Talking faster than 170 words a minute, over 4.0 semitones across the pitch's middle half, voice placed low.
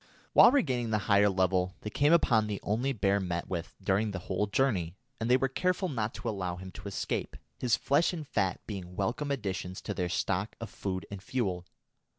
Yes: average, 200 wpm; average, 5.0 semitones; low, 105 Hz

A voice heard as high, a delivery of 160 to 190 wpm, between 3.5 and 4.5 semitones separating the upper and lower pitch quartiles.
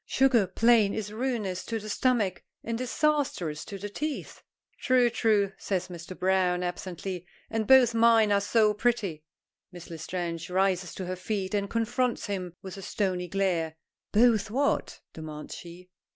No: high, 200 Hz; average, 150 wpm; average, 4.1 semitones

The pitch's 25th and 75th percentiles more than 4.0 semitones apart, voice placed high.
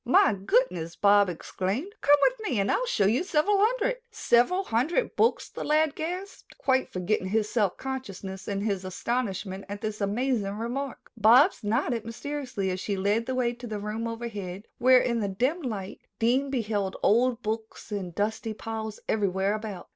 Yes: average, 4.6 semitones; high, 225 Hz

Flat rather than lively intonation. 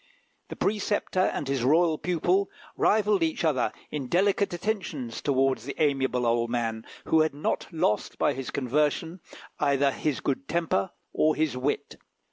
No: average, 4.7 semitones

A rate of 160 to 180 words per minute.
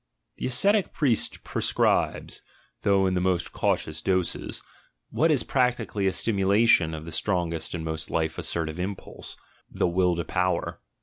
Yes: average, 165 wpm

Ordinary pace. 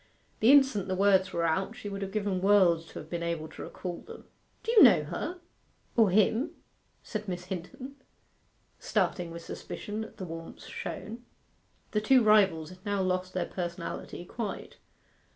Yes: average, 170 wpm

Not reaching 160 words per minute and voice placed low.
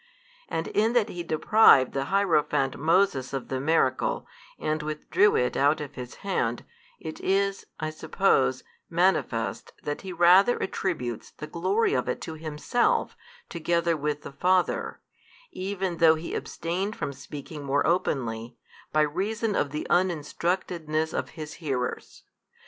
No: average, 140 wpm; medium, 160 Hz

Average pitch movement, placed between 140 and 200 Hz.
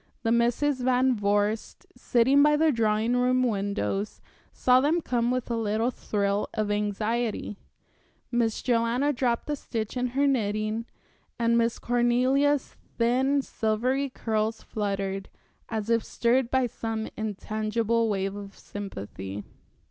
No: average, 3.0 semitones; high, 230 Hz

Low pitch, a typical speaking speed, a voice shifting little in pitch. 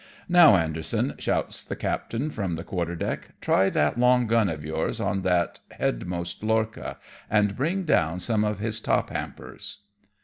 No: low, 105 Hz; average, 160 wpm; average, 4.9 semitones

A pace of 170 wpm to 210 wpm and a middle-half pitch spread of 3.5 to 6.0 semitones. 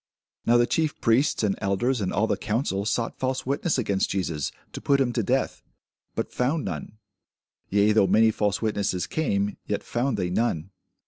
Yes: average, 180 wpm; average, 4.3 semitones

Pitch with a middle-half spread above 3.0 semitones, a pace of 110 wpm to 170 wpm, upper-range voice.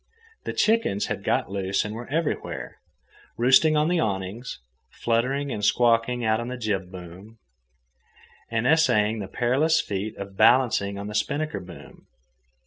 No: average, 4.5 semitones; average, 145 wpm; low, 115 Hz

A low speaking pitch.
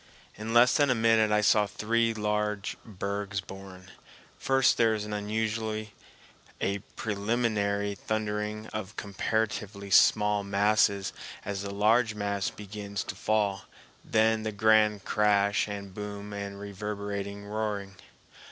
Yes: low, 105 Hz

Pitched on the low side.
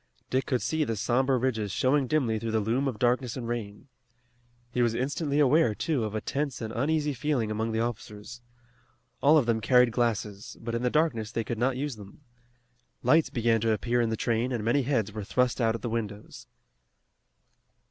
Yes: low, 120 Hz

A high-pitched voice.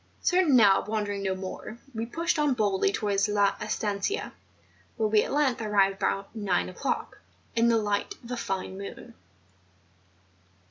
Yes: high, 210 Hz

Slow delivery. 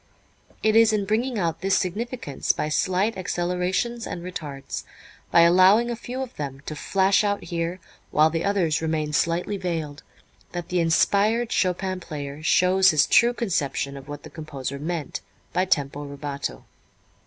No: average, 155 wpm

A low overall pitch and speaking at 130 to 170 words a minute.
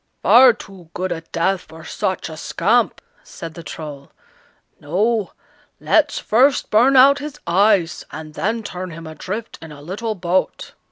No: medium, 185 Hz; average, 155 wpm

